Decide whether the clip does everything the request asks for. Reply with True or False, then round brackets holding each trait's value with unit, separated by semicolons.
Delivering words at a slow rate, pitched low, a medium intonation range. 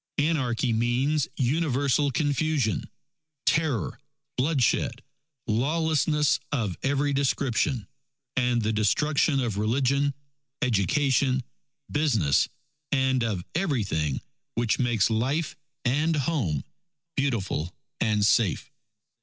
True (85 wpm; 130 Hz; 4.4 semitones)